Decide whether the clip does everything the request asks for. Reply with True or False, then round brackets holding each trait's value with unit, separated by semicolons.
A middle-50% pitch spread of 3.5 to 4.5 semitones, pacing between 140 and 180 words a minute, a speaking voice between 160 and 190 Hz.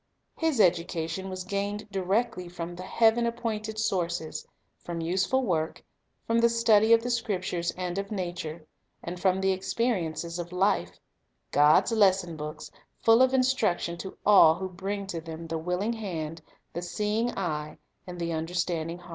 True (4.0 semitones; 160 wpm; 185 Hz)